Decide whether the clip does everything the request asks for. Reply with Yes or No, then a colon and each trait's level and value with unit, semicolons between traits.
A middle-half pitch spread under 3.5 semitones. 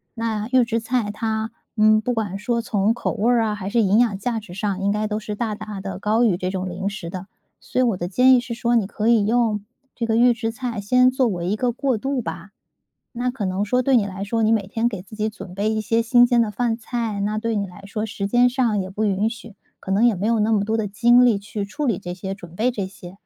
Yes: average, 2.9 semitones